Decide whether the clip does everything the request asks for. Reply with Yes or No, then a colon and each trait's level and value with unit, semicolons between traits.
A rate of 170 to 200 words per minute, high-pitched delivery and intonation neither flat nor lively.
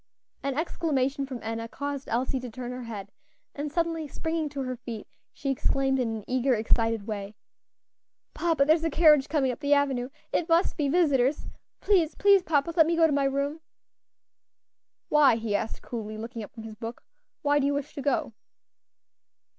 Yes: average, 185 wpm; very high, 275 Hz; average, 4.3 semitones